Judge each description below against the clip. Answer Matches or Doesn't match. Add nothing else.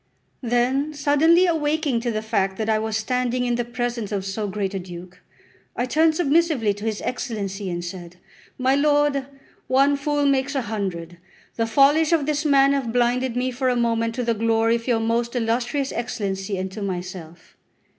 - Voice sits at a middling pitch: Doesn't match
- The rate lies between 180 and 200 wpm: Matches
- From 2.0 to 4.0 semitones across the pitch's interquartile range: Doesn't match